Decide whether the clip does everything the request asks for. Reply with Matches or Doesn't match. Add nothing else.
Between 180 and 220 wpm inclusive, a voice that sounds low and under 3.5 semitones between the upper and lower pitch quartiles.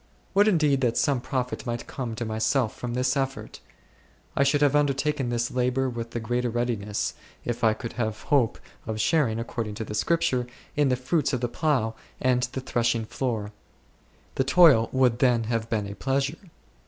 Matches